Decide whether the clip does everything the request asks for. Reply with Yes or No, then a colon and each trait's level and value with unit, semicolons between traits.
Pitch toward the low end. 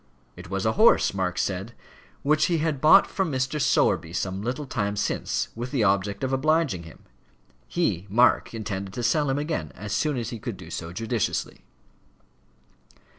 Yes: low, 115 Hz